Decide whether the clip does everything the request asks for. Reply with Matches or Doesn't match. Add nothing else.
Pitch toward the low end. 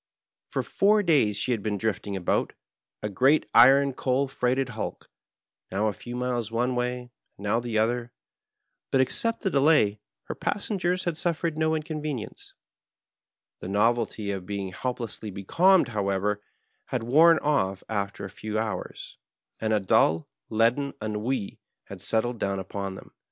Matches